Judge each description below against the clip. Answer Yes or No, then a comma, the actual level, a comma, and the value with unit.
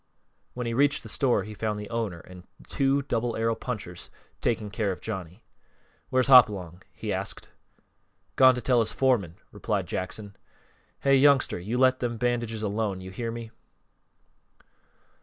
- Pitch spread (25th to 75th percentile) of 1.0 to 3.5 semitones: No, average, 3.9 semitones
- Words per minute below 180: Yes, average, 150 wpm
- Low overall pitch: Yes, low, 115 Hz